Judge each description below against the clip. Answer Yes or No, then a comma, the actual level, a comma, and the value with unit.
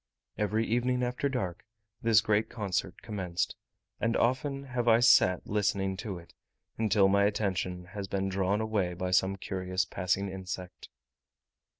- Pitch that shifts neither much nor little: Yes, average, 3.3 semitones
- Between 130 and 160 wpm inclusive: Yes, average, 140 wpm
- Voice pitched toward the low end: Yes, low, 100 Hz